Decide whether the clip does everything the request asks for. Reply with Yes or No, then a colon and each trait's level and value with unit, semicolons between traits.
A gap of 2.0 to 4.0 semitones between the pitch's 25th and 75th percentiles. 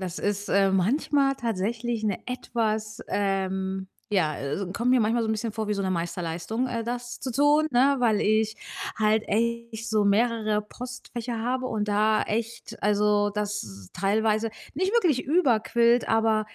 Yes: average, 2.7 semitones